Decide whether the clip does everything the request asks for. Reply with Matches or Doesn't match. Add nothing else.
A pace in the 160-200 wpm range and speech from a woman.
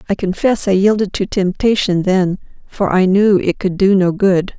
Matches